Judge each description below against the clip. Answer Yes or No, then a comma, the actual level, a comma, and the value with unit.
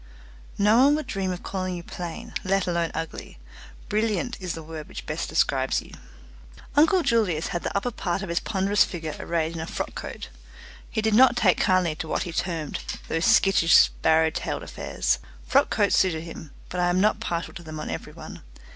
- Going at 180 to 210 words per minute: Yes, average, 200 wpm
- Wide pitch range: No, average, 4.0 semitones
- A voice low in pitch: No, medium, 180 Hz